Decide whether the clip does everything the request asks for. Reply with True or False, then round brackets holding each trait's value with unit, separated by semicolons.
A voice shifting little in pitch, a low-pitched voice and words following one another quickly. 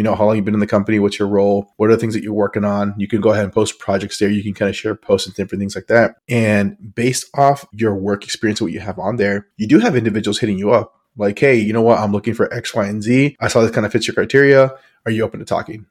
True (2.1 semitones; 105 Hz; 310 wpm)